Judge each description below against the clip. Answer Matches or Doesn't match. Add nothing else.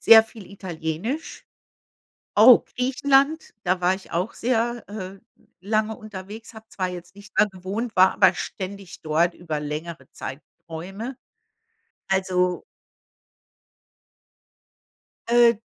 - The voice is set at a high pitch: Matches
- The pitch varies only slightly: Doesn't match